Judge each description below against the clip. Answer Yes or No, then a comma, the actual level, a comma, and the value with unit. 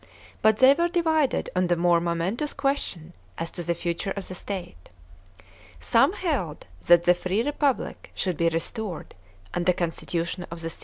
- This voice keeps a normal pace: Yes, average, 170 wpm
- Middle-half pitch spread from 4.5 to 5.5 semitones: Yes, average, 5.0 semitones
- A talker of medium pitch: Yes, medium, 180 Hz